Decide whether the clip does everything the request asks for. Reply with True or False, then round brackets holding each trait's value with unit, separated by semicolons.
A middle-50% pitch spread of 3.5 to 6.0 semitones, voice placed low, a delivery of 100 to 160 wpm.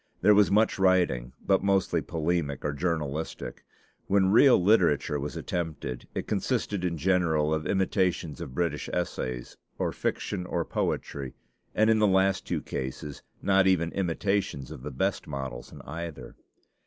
True (4.6 semitones; 85 Hz; 150 wpm)